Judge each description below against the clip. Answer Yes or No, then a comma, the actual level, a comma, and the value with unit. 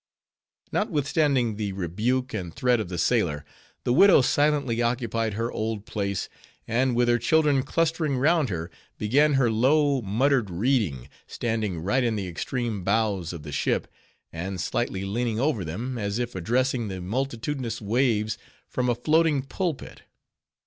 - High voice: No, low, 115 Hz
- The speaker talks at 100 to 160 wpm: Yes, average, 150 wpm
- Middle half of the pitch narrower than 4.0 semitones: No, average, 4.8 semitones